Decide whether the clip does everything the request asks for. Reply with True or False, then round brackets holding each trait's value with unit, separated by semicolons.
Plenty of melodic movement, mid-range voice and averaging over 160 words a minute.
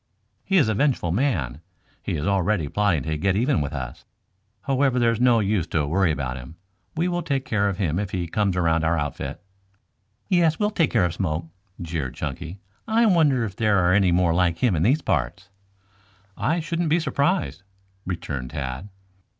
False (8.3 semitones; 95 Hz; 185 wpm)